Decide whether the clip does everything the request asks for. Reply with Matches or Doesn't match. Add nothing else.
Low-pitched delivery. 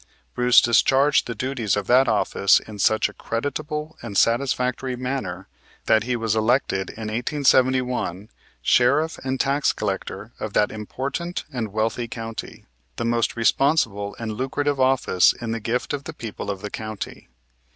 Matches